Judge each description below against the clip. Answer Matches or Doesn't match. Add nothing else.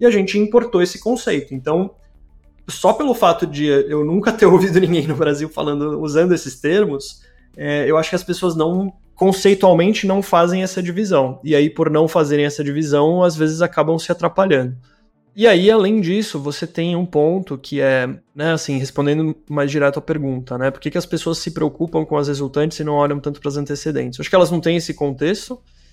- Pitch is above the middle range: Doesn't match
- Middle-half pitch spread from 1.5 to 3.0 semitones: Doesn't match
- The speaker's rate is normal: Doesn't match